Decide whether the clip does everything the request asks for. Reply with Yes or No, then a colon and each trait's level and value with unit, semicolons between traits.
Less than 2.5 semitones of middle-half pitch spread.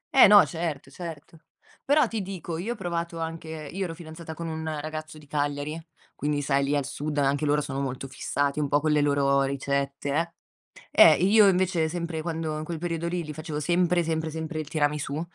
No: average, 2.8 semitones